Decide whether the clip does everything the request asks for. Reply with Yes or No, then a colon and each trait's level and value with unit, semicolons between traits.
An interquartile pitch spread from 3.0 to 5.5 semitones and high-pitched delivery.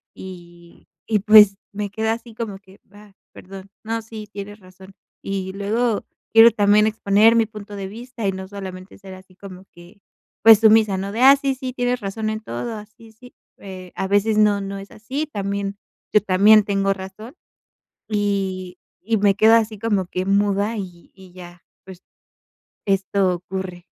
No: narrow, 2.4 semitones; high, 200 Hz